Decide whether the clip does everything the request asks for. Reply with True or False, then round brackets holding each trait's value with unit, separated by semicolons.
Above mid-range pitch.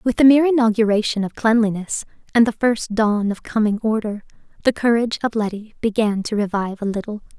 True (220 Hz)